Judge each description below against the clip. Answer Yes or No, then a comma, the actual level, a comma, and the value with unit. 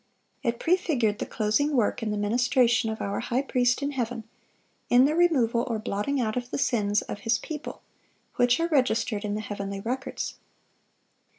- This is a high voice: Yes, high, 240 Hz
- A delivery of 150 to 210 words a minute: Yes, average, 175 wpm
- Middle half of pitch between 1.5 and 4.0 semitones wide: Yes, average, 3.5 semitones